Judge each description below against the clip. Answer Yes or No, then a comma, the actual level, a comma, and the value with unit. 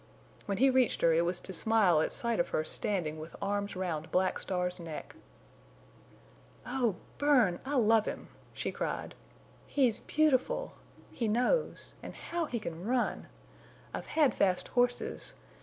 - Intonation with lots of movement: Yes, wide, 5.9 semitones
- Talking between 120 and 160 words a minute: Yes, average, 150 wpm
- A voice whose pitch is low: No, high, 210 Hz